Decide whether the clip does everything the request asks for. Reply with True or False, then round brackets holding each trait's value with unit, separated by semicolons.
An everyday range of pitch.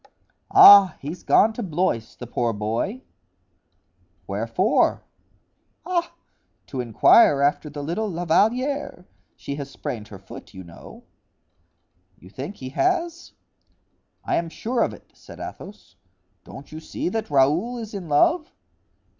False (8.9 semitones)